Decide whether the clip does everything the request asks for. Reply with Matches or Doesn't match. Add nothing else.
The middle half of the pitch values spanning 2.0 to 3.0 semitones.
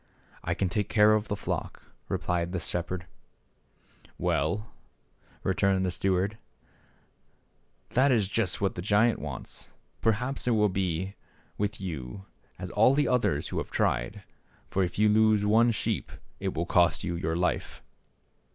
Doesn't match